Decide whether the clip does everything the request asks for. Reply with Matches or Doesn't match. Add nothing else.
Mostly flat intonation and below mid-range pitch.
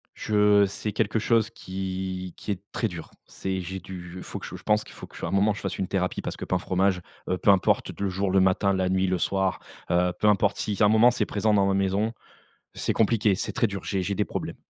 Matches